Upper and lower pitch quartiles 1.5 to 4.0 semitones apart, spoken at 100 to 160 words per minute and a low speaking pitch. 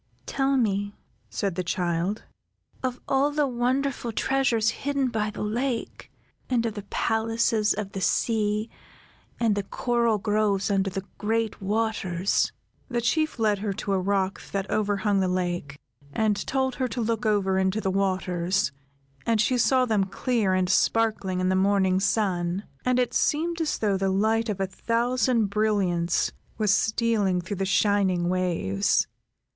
No: average, 3.4 semitones; average, 155 wpm; high, 210 Hz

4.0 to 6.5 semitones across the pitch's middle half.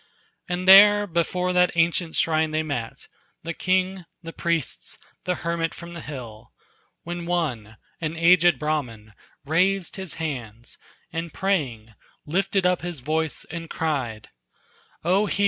No: average, 3.2 semitones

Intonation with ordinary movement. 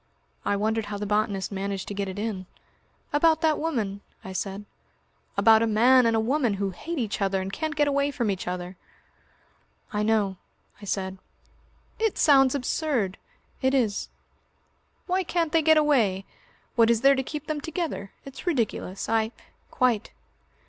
No: wide, 6.3 semitones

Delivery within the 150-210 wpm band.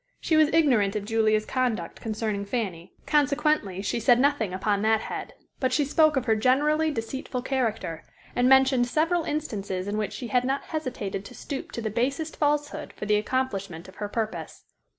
Yes: average, 180 wpm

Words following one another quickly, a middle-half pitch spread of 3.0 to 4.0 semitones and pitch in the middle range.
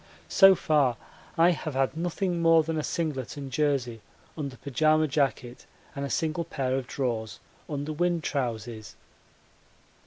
No: average, 145 wpm; average, 3.7 semitones; medium, 145 Hz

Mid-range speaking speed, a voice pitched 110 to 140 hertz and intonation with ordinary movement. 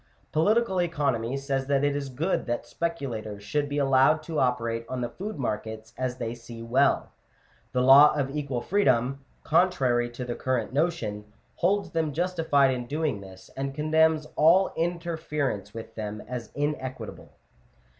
Yes: average, 150 wpm; low, 135 Hz; average, 4.6 semitones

